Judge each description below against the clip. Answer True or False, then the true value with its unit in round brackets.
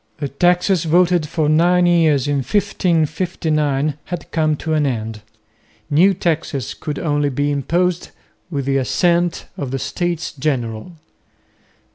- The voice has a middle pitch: True (155 Hz)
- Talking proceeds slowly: True (130 wpm)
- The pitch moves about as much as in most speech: True (3.7 semitones)